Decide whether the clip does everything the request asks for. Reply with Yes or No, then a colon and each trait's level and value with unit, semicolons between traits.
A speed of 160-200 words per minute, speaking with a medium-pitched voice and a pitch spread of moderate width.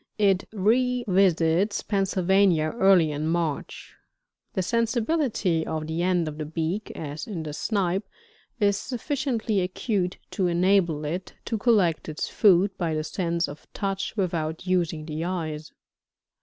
No: slow, 135 wpm; medium, 180 Hz; average, 3.9 semitones